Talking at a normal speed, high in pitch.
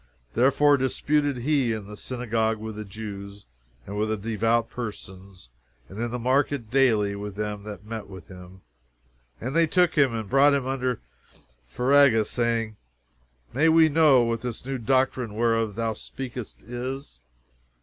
No: average, 155 wpm; low, 115 Hz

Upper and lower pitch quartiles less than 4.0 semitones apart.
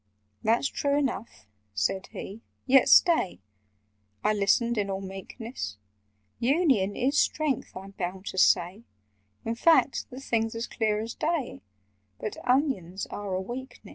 No: wide, 5.4 semitones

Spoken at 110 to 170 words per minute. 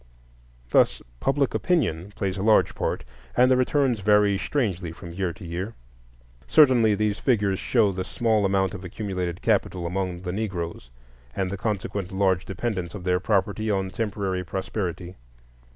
Yes: average, 150 wpm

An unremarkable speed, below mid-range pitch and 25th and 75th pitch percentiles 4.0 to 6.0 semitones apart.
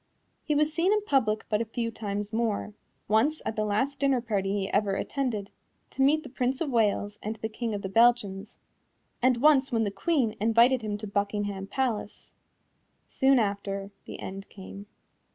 No: average, 180 wpm; high, 220 Hz; average, 4.4 semitones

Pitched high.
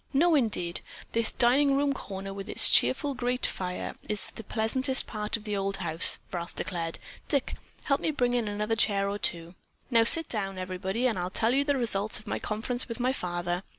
Yes: high, 215 Hz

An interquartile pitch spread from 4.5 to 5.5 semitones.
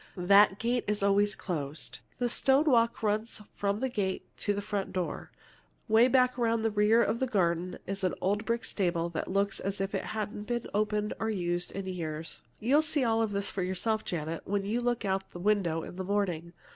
No: average, 3.4 semitones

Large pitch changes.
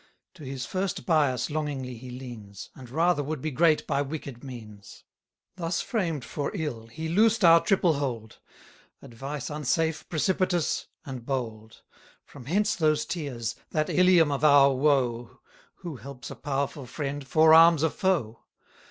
No: average, 4.3 semitones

